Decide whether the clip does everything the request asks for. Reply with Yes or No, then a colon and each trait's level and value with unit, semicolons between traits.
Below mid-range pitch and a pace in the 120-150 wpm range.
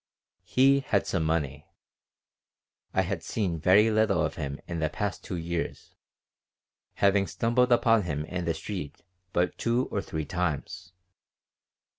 Yes: very low, 90 Hz; average, 140 wpm